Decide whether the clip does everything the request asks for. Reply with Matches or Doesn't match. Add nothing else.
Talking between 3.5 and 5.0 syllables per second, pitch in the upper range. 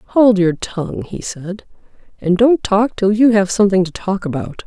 Matches